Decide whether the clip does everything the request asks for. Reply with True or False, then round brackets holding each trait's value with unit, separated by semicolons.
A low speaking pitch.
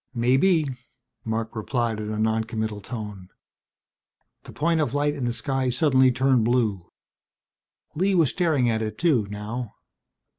True (120 Hz)